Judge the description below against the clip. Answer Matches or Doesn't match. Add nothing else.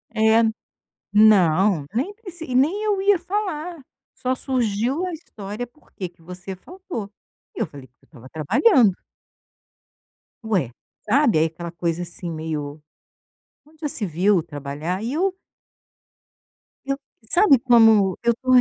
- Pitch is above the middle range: Matches